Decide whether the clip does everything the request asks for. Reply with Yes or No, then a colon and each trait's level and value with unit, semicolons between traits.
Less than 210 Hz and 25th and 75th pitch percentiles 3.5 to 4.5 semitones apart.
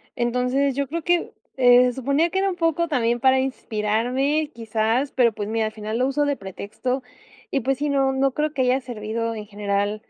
No: very high, 255 Hz; average, 3.8 semitones